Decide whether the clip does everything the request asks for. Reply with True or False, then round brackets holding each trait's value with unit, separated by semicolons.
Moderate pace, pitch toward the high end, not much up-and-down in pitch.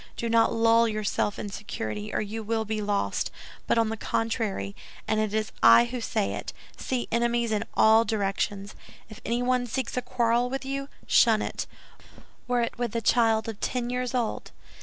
True (175 wpm; 225 Hz; 2.0 semitones)